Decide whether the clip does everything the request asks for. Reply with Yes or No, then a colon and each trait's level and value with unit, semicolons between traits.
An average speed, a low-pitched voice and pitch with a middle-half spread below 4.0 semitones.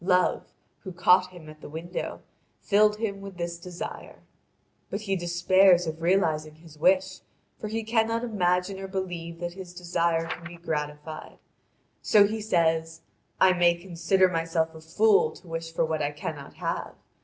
No: average, 165 wpm; medium, 175 Hz; average, 2.7 semitones